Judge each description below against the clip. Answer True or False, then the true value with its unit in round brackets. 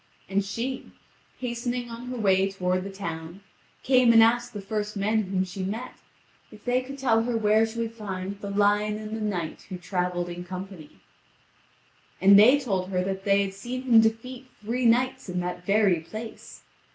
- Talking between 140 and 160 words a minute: False (185 wpm)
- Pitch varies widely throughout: False (3.6 semitones)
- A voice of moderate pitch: False (210 Hz)